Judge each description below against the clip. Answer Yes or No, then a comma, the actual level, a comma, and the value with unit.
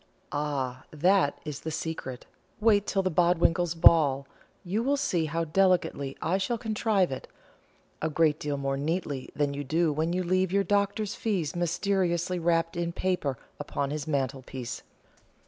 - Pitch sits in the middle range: Yes, medium, 165 Hz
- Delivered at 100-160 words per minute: Yes, average, 155 wpm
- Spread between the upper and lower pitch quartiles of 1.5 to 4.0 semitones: No, average, 4.4 semitones